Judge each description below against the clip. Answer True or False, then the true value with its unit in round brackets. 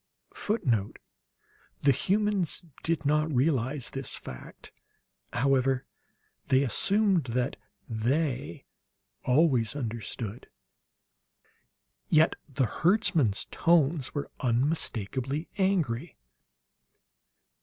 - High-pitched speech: False (135 Hz)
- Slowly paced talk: True (75 wpm)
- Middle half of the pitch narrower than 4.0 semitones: False (5.0 semitones)